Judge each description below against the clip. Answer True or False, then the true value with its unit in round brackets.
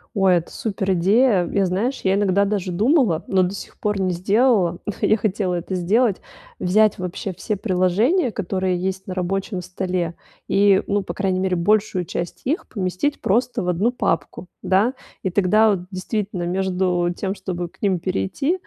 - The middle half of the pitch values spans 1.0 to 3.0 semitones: True (2.6 semitones)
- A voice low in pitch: False (190 Hz)